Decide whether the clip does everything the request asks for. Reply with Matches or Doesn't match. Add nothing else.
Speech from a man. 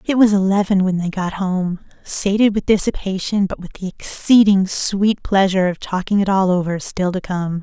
Doesn't match